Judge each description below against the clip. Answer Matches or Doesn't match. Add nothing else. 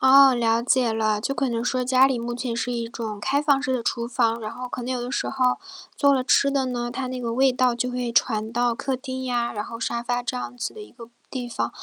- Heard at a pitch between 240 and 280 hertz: Matches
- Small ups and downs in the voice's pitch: Matches